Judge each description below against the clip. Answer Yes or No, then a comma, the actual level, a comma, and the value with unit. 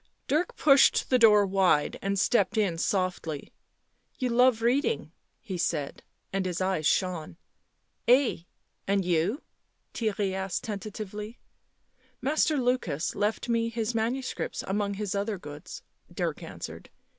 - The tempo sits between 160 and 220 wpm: No, average, 145 wpm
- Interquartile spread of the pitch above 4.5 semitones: No, average, 4.2 semitones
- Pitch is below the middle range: No, high, 205 Hz